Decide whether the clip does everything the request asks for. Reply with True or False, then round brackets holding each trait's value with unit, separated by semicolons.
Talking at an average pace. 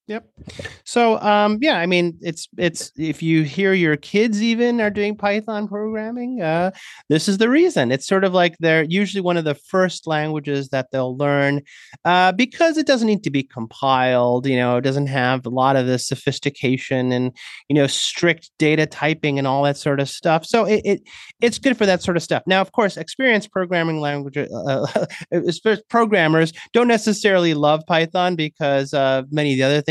True (195 wpm)